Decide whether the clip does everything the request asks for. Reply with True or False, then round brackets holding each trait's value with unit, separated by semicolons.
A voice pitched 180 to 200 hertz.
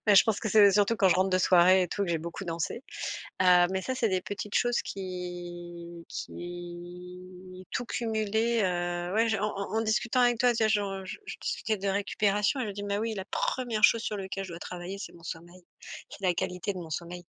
True (190 Hz)